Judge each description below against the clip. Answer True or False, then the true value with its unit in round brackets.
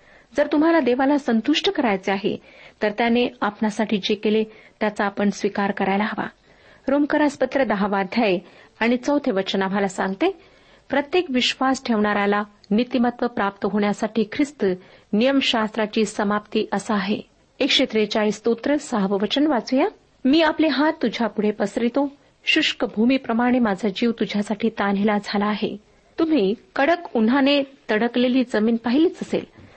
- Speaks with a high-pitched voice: True (225 Hz)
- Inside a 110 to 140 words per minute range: True (125 wpm)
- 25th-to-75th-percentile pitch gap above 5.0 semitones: False (4.6 semitones)